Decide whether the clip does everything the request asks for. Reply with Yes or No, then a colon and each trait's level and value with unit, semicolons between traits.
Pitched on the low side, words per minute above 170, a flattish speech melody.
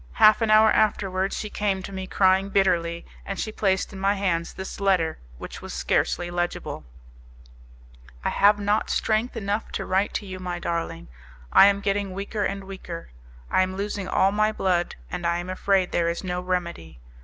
No: high, 190 Hz; average, 185 wpm; narrow, 2.2 semitones